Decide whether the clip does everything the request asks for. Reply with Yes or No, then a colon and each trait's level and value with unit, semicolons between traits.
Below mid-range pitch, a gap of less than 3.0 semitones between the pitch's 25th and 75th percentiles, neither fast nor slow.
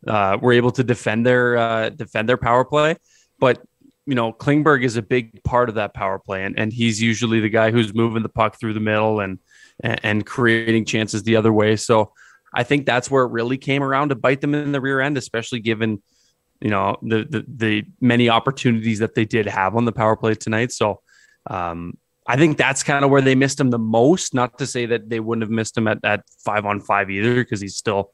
No: low, 115 Hz; narrow, 2.6 semitones; fast, 230 wpm